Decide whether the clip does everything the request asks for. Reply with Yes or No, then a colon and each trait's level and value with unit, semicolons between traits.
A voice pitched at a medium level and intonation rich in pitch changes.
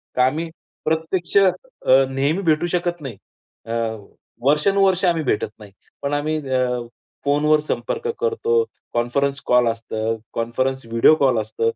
Yes: medium, 145 Hz; wide, 5.7 semitones